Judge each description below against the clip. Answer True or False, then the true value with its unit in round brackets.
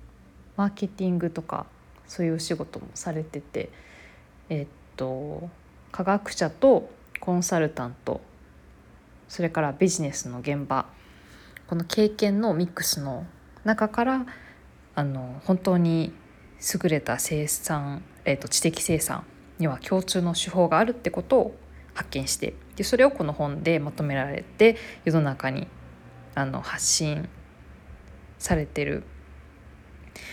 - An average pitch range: False (5.7 semitones)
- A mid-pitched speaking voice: True (160 Hz)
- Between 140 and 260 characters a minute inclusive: True (240 characters per minute)